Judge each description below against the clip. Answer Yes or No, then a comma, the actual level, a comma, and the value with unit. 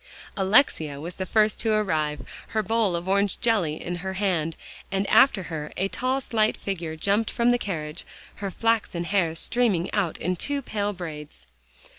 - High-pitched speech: Yes, high, 195 Hz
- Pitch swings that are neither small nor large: Yes, average, 4.6 semitones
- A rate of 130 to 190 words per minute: Yes, average, 170 wpm